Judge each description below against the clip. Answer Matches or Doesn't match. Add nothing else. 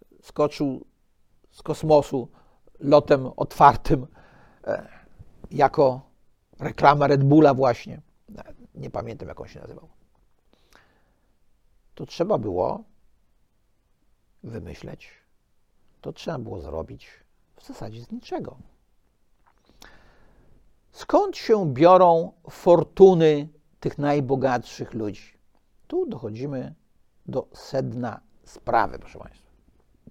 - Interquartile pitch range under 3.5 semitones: Matches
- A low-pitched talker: Doesn't match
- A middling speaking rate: Doesn't match